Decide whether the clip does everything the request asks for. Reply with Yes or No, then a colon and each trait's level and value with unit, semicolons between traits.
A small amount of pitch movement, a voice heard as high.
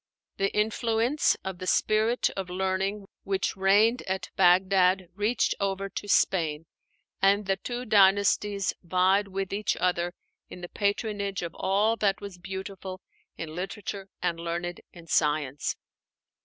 Yes: narrow, 2.1 semitones; high, 195 Hz